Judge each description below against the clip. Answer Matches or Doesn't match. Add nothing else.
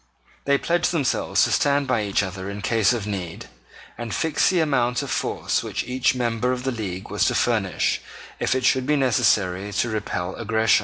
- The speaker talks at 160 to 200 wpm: Matches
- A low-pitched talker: Matches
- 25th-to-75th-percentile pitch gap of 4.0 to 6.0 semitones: Matches